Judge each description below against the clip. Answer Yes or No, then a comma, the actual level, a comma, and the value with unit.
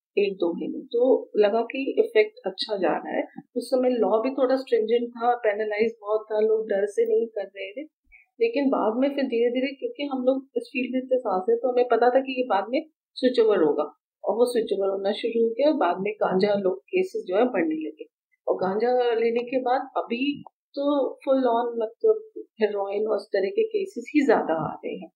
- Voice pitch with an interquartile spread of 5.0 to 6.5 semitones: Yes, average, 5.3 semitones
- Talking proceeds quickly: Yes, fast, 220 wpm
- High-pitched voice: Yes, very high, 250 Hz